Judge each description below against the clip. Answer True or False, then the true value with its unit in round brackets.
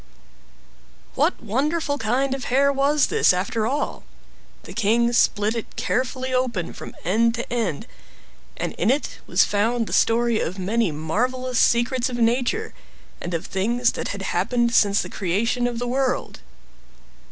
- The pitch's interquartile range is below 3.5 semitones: True (3.1 semitones)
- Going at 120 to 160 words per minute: True (150 wpm)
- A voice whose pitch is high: True (235 Hz)